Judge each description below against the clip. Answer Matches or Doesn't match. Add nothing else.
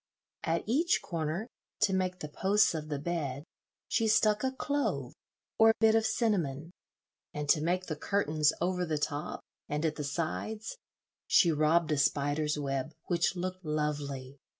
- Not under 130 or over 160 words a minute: Matches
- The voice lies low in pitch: Doesn't match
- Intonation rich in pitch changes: Doesn't match